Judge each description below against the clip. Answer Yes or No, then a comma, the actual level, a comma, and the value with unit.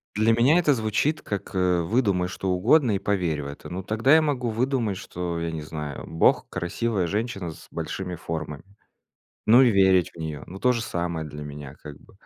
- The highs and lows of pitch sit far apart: Yes, wide, 5.7 semitones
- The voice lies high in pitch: No, very low, 95 Hz